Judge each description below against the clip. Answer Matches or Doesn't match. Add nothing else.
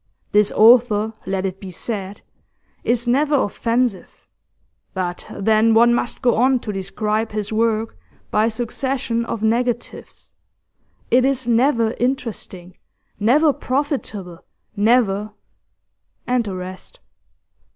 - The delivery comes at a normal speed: Doesn't match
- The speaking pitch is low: Doesn't match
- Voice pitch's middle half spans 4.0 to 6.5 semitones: Doesn't match